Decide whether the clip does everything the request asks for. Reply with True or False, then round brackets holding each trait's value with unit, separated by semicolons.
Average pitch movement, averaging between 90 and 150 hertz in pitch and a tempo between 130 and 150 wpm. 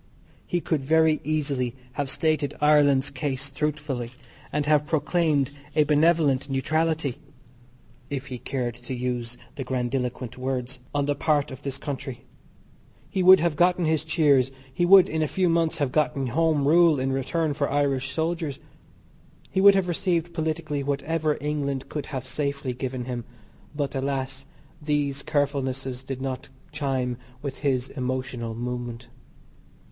True (3.0 semitones; 140 Hz; 145 wpm)